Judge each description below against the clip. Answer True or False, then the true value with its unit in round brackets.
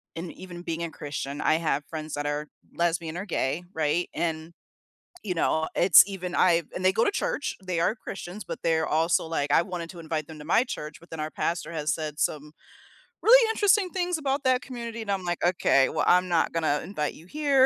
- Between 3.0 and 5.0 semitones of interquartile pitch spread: True (3.7 semitones)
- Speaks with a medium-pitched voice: True (170 Hz)